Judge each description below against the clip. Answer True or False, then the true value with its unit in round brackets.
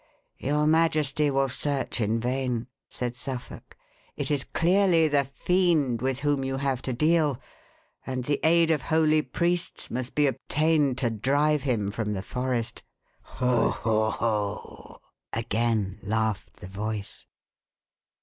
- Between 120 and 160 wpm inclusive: True (135 wpm)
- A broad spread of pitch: False (4.6 semitones)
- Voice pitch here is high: False (130 Hz)